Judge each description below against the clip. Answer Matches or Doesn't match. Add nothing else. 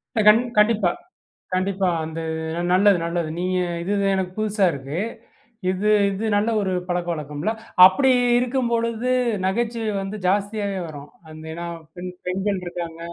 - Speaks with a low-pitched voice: Doesn't match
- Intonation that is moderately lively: Matches